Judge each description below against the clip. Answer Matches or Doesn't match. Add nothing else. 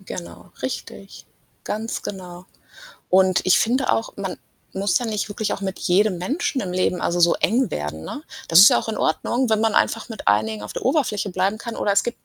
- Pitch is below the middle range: Doesn't match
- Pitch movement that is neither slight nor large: Matches